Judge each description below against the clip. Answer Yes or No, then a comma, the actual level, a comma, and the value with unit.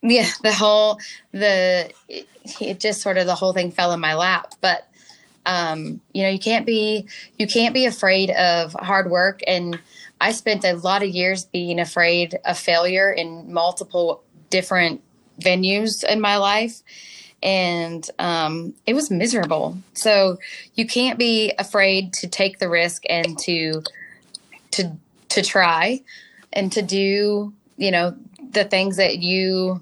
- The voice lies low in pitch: No, high, 190 Hz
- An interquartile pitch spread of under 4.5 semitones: Yes, average, 3.1 semitones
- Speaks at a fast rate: No, average, 155 wpm